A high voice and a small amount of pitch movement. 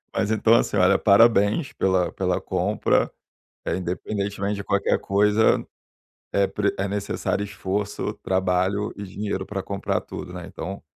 No: low, 100 Hz; narrow, 1.6 semitones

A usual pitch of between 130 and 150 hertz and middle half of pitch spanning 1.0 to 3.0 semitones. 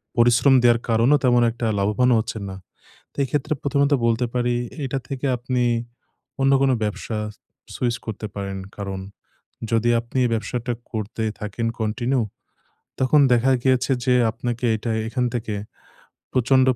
No: low, 120 Hz; narrow, 2.6 semitones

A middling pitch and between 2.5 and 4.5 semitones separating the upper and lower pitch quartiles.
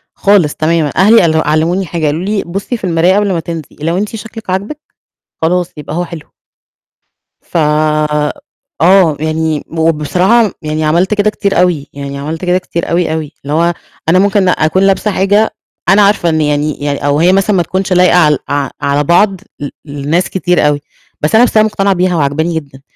Yes: medium, 170 Hz; average, 3.9 semitones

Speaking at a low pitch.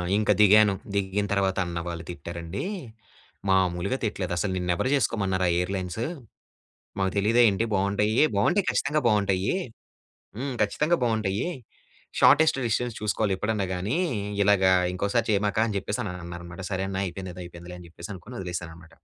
Yes: low, 100 Hz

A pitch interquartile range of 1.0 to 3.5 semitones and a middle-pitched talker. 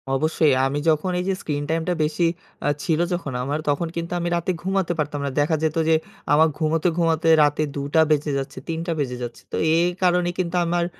Yes: average, 2.8 semitones; medium, 160 Hz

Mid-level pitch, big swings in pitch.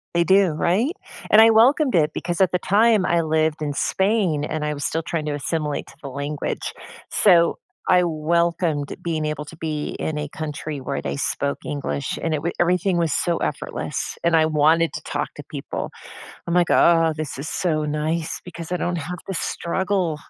No: medium, 165 Hz; average, 2.8 semitones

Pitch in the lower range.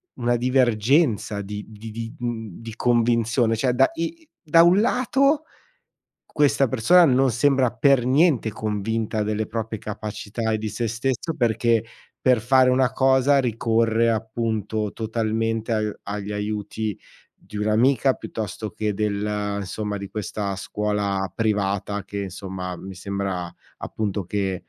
Yes: low, 110 Hz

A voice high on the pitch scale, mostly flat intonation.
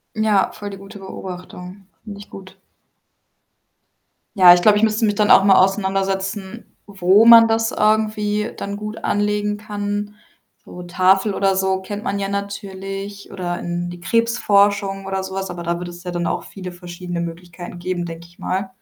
Yes: high, 195 Hz; narrow, 2.3 semitones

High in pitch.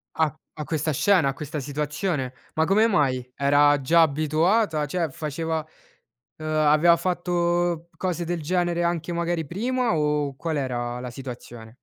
No: medium, 155 Hz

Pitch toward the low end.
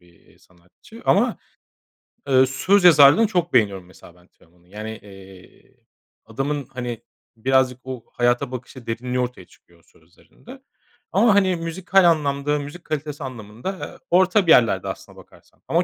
Yes: low, 130 Hz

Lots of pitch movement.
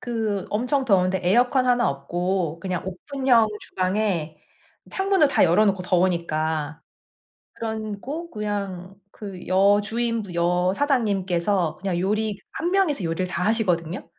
No: average, 4.3 semitones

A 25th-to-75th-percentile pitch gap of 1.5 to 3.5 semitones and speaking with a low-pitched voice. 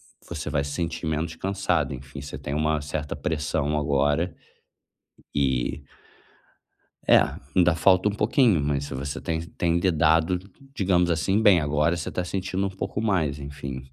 No: average, 3.9 semitones; very low, 80 Hz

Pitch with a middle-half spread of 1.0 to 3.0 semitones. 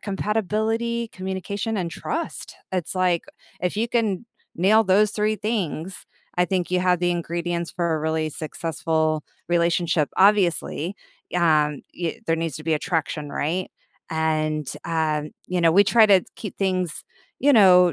No: average, 3.8 semitones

